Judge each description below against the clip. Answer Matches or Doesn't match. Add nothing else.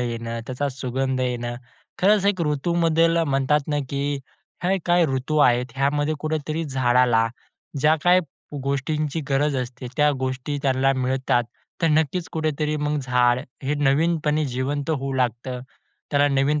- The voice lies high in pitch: Doesn't match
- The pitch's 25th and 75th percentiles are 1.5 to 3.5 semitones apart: Matches